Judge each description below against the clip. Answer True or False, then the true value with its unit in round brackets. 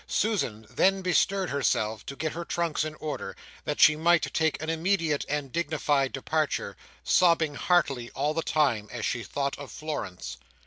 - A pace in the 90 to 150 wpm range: False (165 wpm)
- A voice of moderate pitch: True (150 Hz)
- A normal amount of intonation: True (3.6 semitones)